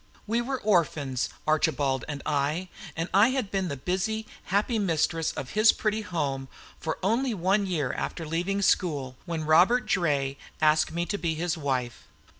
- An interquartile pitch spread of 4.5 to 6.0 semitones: Yes, average, 5.2 semitones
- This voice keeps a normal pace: Yes, average, 165 wpm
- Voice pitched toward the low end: No, medium, 170 Hz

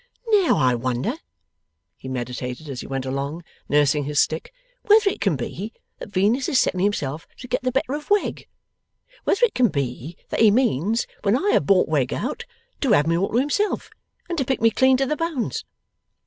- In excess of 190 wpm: Yes, average, 200 wpm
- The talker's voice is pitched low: No, high, 200 Hz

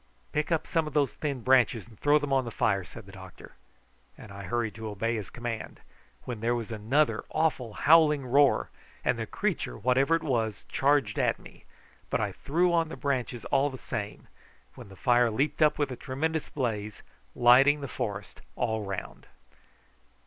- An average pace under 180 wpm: No, average, 185 wpm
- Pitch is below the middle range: Yes, low, 125 Hz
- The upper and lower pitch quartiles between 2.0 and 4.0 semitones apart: No, average, 4.8 semitones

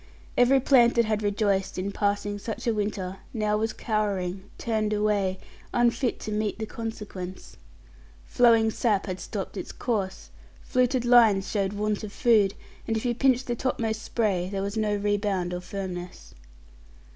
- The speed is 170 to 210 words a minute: No, average, 155 wpm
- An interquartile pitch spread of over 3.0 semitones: No, narrow, 2.6 semitones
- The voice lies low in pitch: No, high, 210 Hz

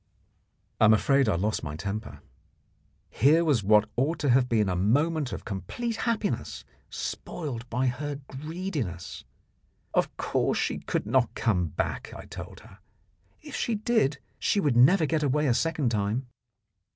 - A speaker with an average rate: Yes, average, 155 wpm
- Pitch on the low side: Yes, low, 130 Hz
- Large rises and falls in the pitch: Yes, wide, 6.4 semitones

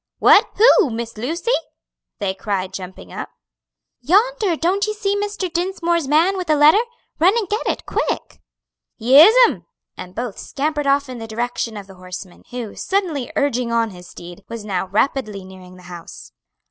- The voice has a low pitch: No, very high, 255 Hz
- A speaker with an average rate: Yes, average, 165 wpm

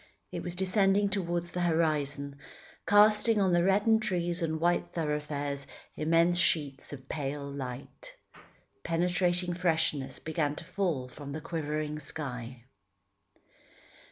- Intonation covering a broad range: No, average, 3.7 semitones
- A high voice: No, medium, 165 Hz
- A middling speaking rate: No, slow, 120 wpm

